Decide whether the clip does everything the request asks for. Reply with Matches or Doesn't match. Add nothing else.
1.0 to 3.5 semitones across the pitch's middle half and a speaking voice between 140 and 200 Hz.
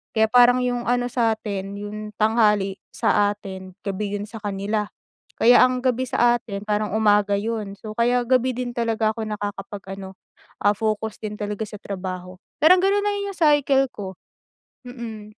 Doesn't match